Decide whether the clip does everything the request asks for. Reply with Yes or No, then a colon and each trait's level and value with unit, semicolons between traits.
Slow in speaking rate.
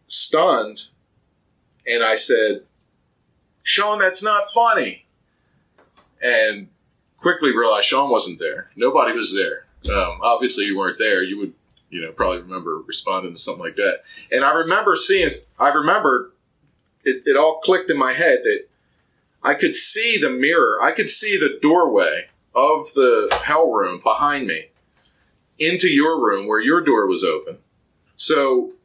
No: average, 150 wpm